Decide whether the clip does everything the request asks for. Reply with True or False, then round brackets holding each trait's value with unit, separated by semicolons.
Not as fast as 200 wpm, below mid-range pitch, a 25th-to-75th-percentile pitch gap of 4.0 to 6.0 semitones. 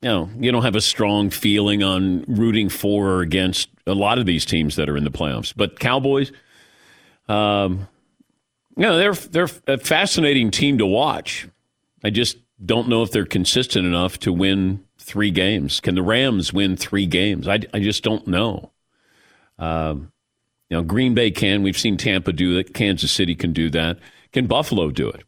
False (190 wpm; 100 Hz; 3.5 semitones)